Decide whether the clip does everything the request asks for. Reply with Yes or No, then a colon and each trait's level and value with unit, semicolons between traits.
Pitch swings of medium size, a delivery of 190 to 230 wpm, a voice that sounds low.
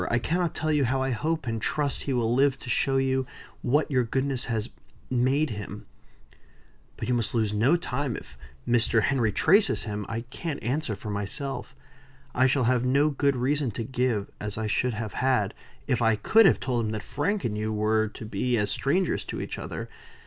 Yes: average, 4.0 semitones; average, 200 wpm; low, 125 Hz